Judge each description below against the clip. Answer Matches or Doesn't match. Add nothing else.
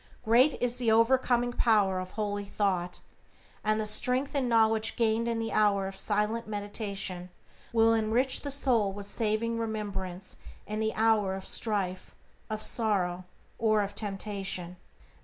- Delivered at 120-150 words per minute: Matches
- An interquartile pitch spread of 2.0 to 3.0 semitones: Matches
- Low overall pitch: Doesn't match